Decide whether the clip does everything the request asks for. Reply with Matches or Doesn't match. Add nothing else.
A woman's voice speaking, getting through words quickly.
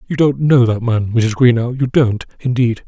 Doesn't match